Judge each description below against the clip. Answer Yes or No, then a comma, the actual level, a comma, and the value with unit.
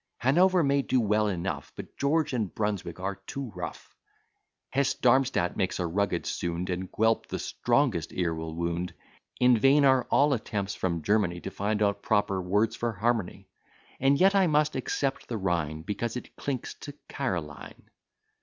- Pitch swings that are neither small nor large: No, wide, 6.7 semitones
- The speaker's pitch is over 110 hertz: No, low, 105 Hz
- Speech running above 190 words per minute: No, average, 165 wpm